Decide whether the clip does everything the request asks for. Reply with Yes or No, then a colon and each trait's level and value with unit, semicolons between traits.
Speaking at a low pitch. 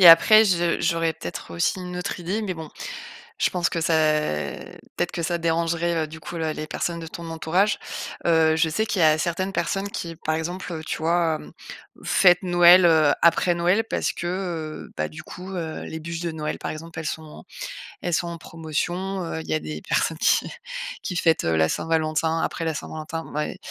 No: medium, 165 Hz